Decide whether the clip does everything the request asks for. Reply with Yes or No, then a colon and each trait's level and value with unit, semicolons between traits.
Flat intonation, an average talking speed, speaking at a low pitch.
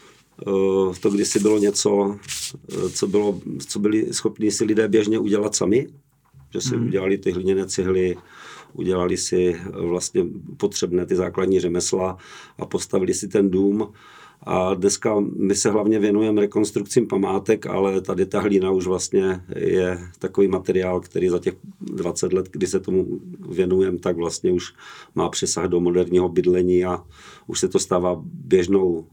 Yes: narrow, 2.3 semitones; average, 150 wpm; very low, 95 Hz